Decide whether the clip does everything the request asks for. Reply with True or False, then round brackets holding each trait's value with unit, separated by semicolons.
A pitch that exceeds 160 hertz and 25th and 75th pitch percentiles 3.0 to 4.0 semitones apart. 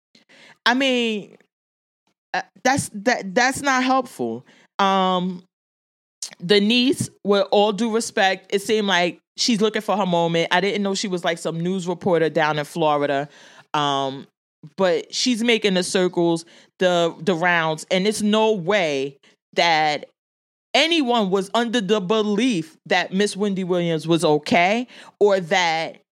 False (190 Hz; 4.7 semitones)